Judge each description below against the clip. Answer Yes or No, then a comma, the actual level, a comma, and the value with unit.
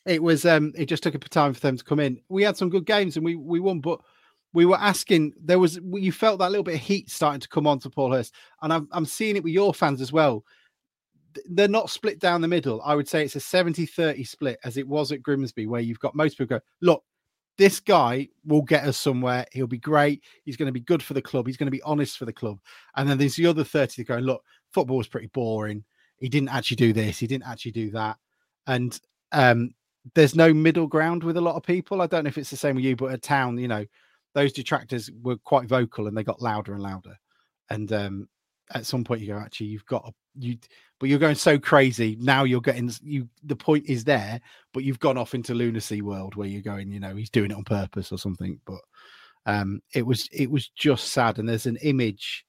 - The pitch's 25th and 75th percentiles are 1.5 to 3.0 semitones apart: No, average, 5.0 semitones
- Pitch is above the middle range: No, low, 135 Hz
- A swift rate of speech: Yes, fast, 250 wpm